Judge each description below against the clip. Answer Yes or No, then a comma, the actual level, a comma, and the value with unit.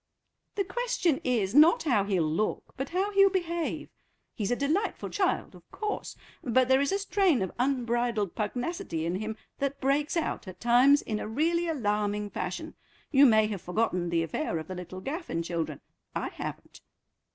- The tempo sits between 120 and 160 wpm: No, average, 175 wpm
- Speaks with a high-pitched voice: Yes, high, 245 Hz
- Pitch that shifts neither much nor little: No, wide, 8.0 semitones